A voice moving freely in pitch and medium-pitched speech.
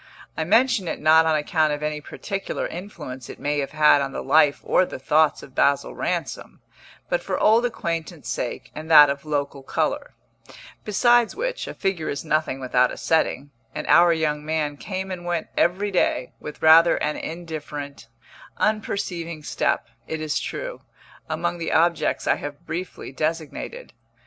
No: average, 3.5 semitones; medium, 160 Hz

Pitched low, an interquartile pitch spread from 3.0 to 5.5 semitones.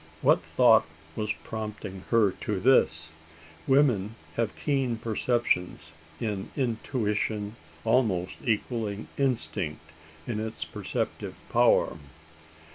Yes: low, 110 Hz; average, 3.5 semitones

